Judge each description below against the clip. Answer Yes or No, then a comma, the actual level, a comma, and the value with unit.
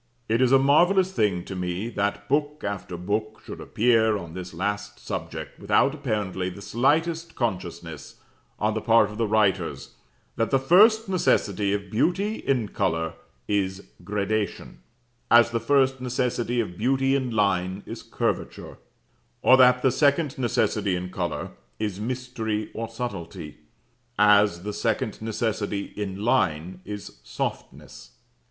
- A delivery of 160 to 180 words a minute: No, average, 140 wpm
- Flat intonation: No, average, 4.6 semitones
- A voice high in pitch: No, low, 110 Hz